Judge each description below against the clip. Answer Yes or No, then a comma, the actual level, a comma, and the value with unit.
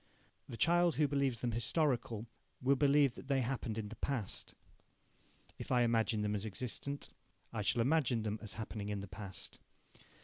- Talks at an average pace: Yes, average, 170 wpm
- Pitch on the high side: No, low, 120 Hz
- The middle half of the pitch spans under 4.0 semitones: No, average, 4.4 semitones